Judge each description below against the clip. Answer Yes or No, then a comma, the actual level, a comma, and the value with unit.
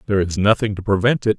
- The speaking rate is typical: No, fast, 260 wpm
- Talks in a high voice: No, low, 105 Hz